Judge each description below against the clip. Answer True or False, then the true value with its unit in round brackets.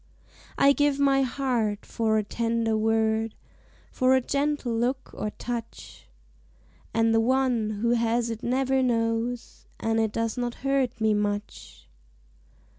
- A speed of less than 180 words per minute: True (135 wpm)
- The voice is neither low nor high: False (230 Hz)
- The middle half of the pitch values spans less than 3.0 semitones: True (2.6 semitones)